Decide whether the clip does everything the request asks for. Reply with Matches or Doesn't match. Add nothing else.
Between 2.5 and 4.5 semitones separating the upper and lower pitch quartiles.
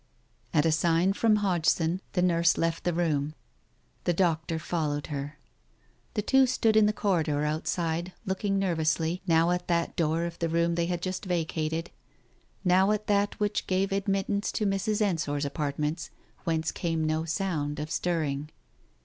Matches